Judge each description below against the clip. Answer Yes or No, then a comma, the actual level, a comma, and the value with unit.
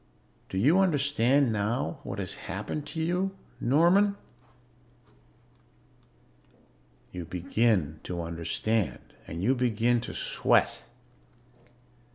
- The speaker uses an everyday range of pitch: No, wide, 7.9 semitones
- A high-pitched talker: No, low, 120 Hz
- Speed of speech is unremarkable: No, slow, 95 wpm